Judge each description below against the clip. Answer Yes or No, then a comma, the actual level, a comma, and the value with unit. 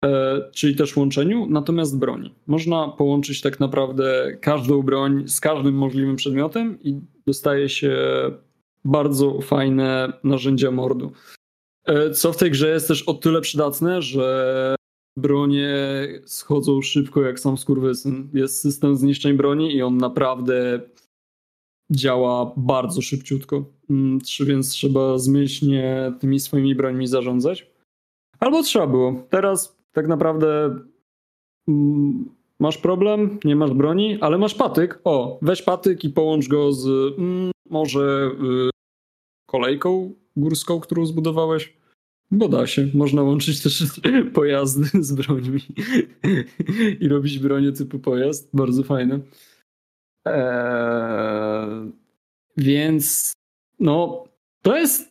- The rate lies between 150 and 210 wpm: No, average, 115 wpm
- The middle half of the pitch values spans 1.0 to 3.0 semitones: Yes, average, 2.7 semitones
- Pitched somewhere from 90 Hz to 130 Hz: No, medium, 140 Hz